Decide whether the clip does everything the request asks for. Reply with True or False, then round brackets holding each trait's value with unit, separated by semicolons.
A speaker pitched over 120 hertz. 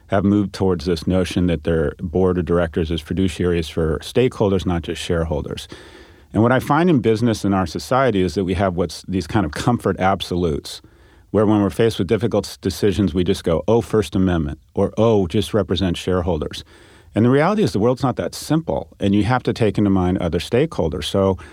False (95 Hz)